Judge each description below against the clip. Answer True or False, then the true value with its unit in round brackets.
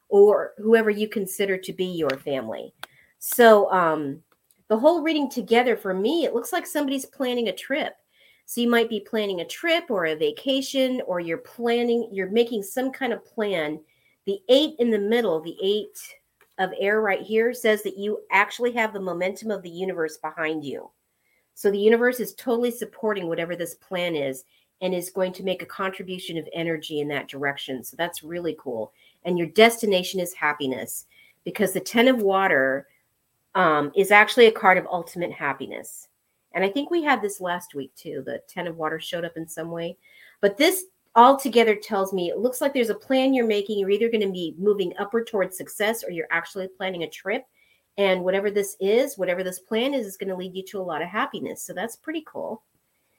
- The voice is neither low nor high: False (195 Hz)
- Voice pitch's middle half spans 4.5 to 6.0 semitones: True (5.0 semitones)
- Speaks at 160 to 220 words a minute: True (200 wpm)